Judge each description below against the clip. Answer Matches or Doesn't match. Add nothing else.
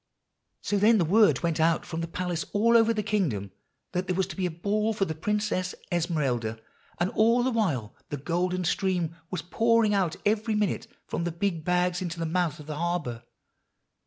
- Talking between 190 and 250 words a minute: Matches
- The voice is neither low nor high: Matches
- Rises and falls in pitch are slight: Doesn't match